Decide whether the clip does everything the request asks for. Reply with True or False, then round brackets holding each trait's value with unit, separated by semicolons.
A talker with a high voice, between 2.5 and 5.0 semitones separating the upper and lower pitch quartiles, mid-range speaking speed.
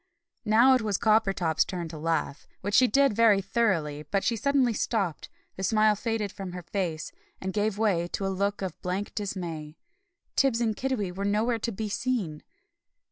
True (205 Hz; 3.7 semitones; 180 wpm)